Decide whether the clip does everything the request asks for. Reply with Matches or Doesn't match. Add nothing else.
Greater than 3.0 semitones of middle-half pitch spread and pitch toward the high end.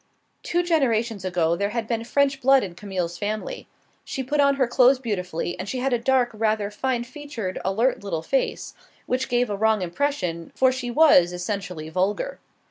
Matches